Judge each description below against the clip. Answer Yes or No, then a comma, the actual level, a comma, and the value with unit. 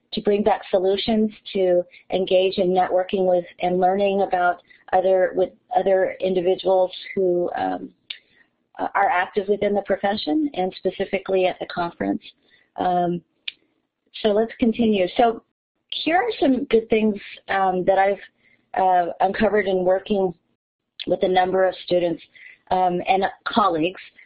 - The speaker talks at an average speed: No, slow, 130 wpm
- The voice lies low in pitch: No, high, 190 Hz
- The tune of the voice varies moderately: No, narrow, 2.1 semitones